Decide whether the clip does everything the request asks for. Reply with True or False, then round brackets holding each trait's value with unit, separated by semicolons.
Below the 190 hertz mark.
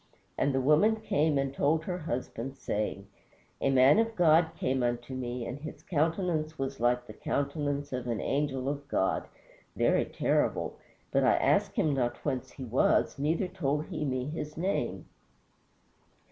True (140 Hz)